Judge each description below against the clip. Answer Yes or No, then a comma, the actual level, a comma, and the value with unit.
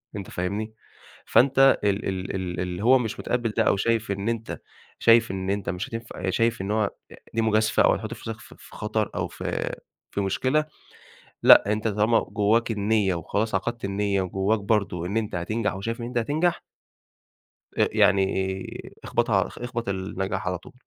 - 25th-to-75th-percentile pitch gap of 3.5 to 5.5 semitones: No, average, 3.0 semitones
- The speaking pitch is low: Yes, low, 105 Hz